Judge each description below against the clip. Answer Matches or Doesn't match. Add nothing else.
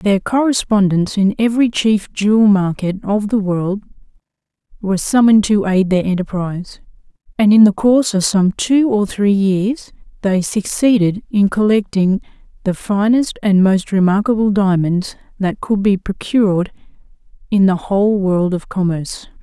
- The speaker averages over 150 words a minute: Doesn't match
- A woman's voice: Matches